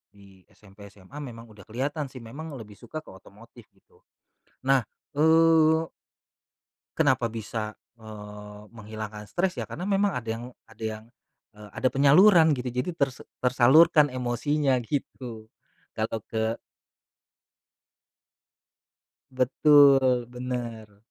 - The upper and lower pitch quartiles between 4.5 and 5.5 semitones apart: Yes, average, 4.9 semitones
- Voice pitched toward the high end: No, low, 125 Hz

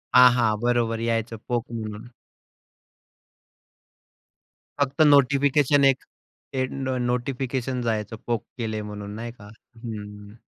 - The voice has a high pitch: No, low, 120 Hz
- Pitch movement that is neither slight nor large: Yes, average, 3.0 semitones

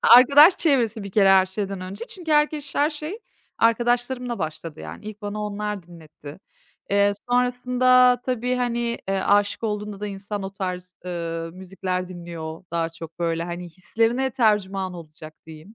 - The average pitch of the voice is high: Yes, high, 205 Hz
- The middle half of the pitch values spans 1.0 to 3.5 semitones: No, average, 5.3 semitones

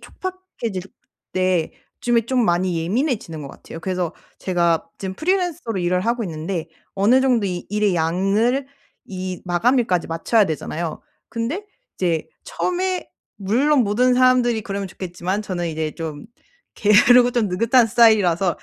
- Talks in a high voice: Yes, high, 200 Hz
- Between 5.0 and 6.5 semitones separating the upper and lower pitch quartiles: Yes, wide, 5.6 semitones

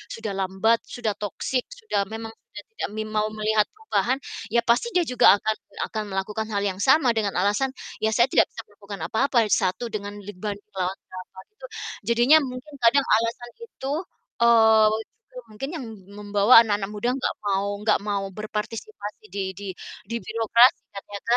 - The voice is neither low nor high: No, high, 220 Hz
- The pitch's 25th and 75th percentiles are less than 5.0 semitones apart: Yes, average, 3.1 semitones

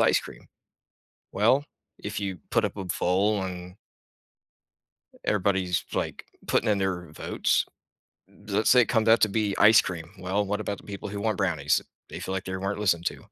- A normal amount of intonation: No, narrow, 2.3 semitones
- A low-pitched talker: Yes, low, 100 Hz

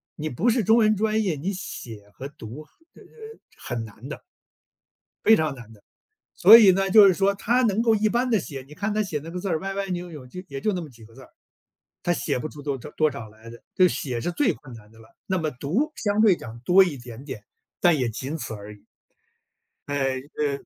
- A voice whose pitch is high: No, medium, 155 Hz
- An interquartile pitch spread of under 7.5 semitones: No, wide, 7.9 semitones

